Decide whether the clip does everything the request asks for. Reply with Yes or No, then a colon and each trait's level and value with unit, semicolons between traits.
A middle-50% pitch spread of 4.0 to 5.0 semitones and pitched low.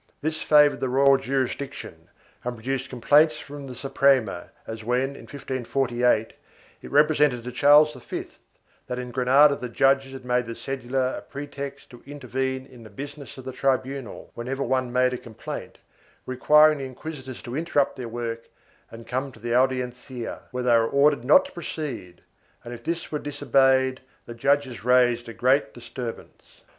No: narrow, 2.4 semitones; low, 130 Hz